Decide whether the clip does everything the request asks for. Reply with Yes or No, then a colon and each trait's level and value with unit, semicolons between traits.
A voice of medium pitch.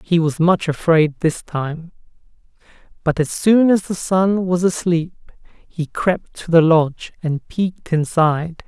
Yes: medium, 165 Hz